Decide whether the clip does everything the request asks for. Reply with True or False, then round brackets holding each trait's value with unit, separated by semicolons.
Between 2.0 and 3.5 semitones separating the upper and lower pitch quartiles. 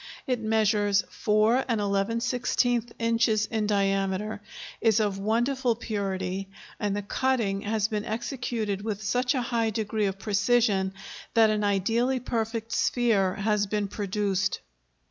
True (2.4 semitones)